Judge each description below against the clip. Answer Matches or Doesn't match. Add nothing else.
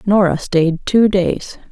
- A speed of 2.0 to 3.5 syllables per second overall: Matches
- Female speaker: Matches